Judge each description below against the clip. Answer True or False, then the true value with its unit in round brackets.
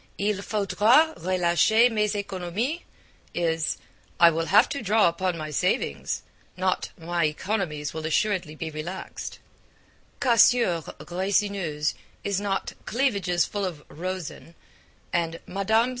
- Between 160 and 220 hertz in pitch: True (185 Hz)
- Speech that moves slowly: True (115 wpm)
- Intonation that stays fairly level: False (4.1 semitones)